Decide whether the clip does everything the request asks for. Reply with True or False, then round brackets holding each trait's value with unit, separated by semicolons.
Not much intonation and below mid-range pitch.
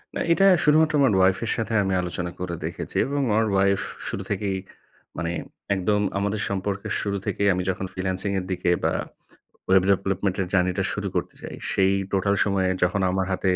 True (1.5 semitones; 95 Hz)